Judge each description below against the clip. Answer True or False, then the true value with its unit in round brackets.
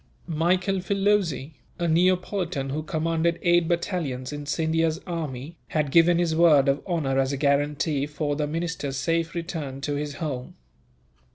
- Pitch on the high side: False (160 Hz)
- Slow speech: False (150 wpm)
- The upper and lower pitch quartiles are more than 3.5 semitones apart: False (3.2 semitones)